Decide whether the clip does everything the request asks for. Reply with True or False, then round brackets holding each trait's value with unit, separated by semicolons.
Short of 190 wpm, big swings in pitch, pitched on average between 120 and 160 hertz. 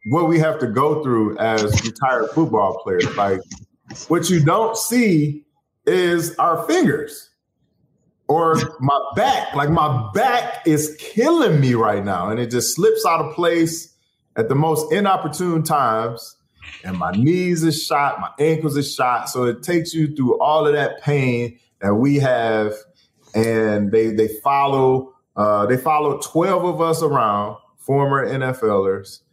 True (155 wpm; 6.0 semitones; 140 Hz)